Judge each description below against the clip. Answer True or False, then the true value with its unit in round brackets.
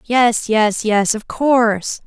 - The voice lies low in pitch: False (225 Hz)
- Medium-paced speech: True (145 wpm)